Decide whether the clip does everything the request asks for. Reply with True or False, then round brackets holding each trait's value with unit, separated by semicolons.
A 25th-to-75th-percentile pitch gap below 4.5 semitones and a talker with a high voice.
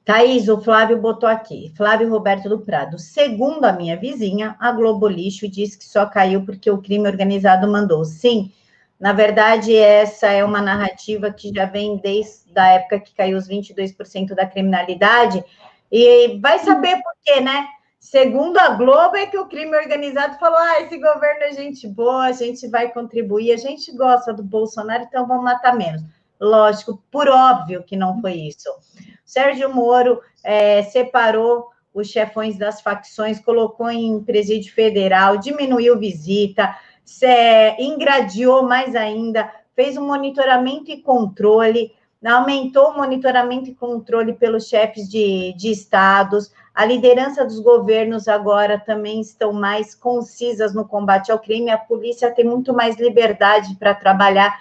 True (3.4 semitones; 220 Hz)